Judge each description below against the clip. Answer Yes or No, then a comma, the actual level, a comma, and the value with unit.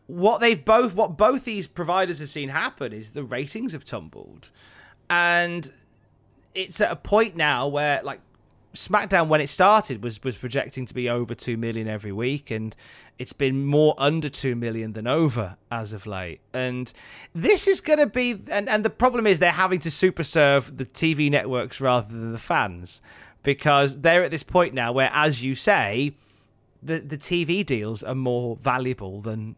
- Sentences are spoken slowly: No, average, 185 wpm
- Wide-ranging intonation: Yes, wide, 6.6 semitones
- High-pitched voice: No, medium, 140 Hz